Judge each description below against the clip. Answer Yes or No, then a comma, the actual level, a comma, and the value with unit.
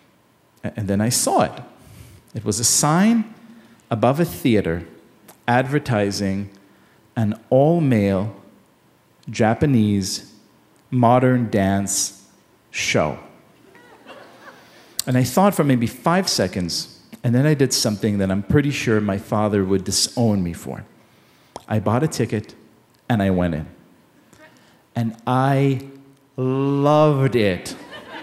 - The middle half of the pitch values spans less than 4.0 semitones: No, average, 5.2 semitones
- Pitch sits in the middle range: No, low, 115 Hz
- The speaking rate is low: Yes, slow, 115 wpm